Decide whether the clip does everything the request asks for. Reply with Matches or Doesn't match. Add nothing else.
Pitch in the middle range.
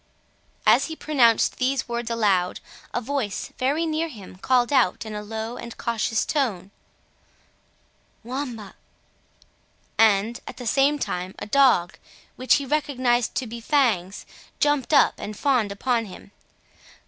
Doesn't match